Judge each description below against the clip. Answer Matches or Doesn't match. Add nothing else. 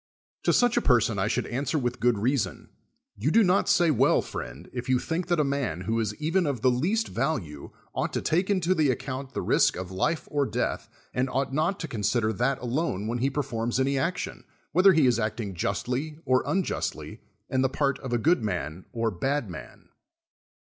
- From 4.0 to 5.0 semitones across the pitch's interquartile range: Doesn't match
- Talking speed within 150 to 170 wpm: Doesn't match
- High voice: Doesn't match